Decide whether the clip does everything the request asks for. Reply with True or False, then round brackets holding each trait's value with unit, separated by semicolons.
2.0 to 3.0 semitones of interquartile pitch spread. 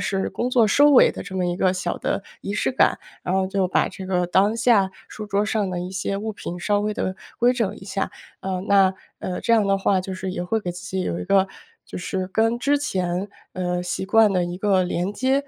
True (2.6 semitones)